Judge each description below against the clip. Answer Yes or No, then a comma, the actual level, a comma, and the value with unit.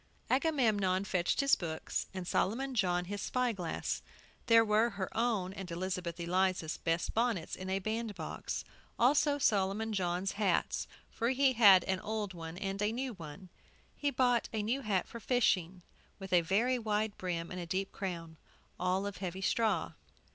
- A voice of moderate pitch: No, high, 195 Hz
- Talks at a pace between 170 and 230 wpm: No, average, 160 wpm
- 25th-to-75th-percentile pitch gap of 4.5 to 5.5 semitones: No, average, 3.9 semitones